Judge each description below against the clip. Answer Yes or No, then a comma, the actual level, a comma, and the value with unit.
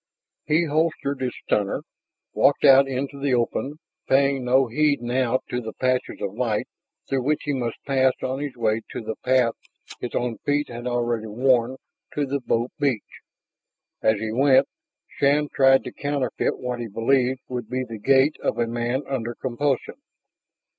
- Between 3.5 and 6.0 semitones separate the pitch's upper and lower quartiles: No, average, 2.7 semitones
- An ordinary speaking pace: Yes, average, 165 wpm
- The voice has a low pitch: Yes, low, 130 Hz